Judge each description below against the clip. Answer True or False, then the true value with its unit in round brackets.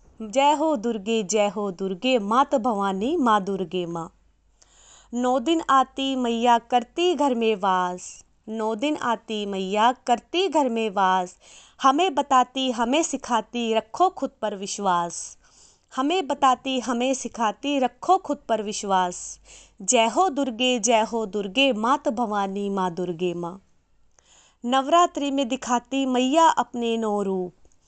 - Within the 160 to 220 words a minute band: False (130 wpm)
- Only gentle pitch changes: False (4.9 semitones)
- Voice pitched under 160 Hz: False (235 Hz)